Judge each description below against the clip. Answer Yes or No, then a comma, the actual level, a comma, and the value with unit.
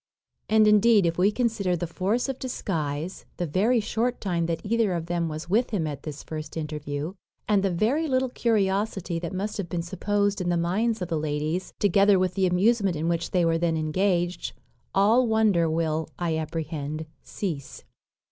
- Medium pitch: Yes, medium, 180 Hz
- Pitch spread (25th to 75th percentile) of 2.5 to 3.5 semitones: No, average, 4.3 semitones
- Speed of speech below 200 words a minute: Yes, average, 185 wpm